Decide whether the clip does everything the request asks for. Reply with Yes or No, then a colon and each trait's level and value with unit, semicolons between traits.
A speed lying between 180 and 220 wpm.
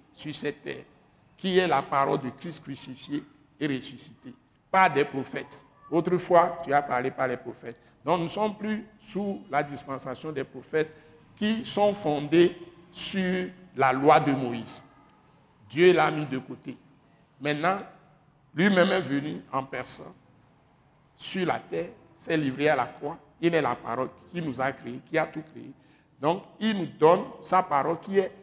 No: average, 165 wpm